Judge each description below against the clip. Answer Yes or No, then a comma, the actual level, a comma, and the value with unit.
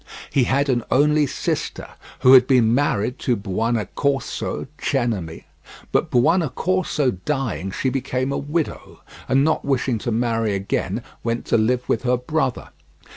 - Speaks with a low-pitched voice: Yes, low, 125 Hz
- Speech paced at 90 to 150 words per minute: Yes, average, 140 wpm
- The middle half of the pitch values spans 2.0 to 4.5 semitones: Yes, average, 3.3 semitones